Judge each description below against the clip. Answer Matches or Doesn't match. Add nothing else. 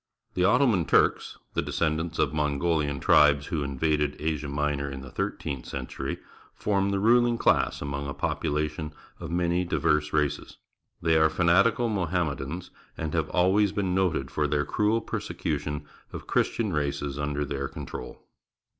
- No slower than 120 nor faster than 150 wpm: Matches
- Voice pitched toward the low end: Matches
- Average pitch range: Matches